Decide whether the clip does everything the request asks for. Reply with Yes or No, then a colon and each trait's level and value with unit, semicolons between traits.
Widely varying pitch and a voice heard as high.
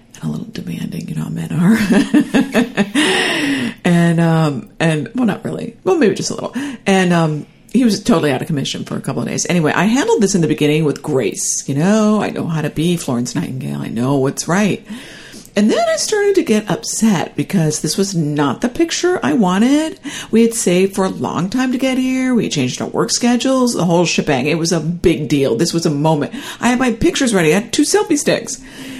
Yes: wide, 7.9 semitones; high, 205 Hz